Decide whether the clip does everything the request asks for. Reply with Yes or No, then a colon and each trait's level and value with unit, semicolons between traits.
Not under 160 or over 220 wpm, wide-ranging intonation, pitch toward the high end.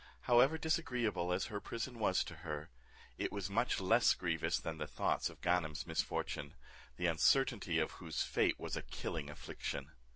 No: average, 165 wpm; wide, 6.4 semitones; very low, 90 Hz